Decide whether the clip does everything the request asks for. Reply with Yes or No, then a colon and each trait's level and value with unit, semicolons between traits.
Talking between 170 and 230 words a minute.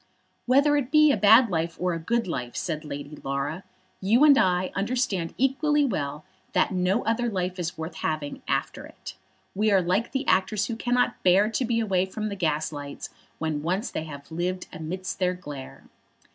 Yes: average, 185 wpm